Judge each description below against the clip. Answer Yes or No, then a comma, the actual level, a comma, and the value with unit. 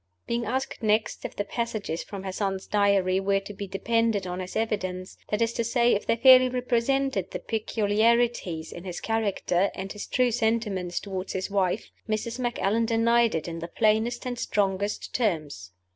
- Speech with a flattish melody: No, average, 3.6 semitones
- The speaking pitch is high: Yes, high, 210 Hz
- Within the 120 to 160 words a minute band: No, average, 175 wpm